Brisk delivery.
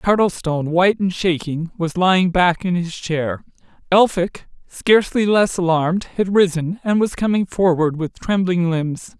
No: average, 150 wpm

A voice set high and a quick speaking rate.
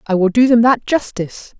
Yes: high, 220 Hz; fast, 225 wpm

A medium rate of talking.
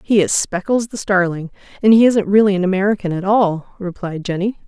Yes: average, 190 wpm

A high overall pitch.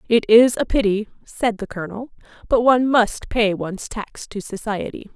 Yes: high, 220 Hz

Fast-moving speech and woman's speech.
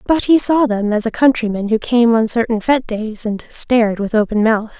Yes: fast, 225 wpm; female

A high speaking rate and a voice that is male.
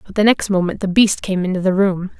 No: fast, 275 wpm; female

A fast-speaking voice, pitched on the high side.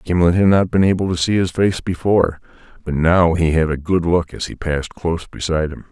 No: fast, 235 wpm; very low, 85 Hz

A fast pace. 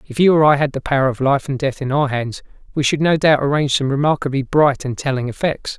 Yes: fast, 260 wpm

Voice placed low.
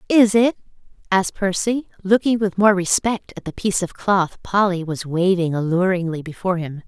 No: high, 190 Hz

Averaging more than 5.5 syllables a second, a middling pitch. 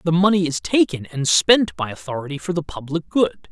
No: 5.3 syllables/s; medium, 160 Hz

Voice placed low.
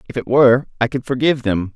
Yes: low, 120 Hz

